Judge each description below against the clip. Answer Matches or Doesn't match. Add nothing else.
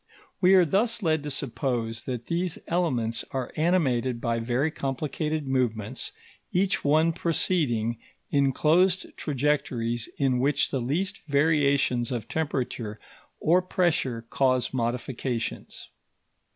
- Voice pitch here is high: Doesn't match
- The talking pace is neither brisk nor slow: Doesn't match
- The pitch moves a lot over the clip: Doesn't match